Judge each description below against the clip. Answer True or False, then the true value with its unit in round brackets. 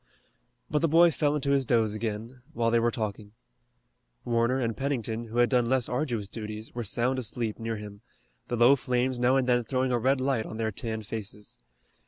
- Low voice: True (120 Hz)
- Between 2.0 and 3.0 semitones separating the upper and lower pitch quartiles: True (2.7 semitones)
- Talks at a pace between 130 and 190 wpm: False (200 wpm)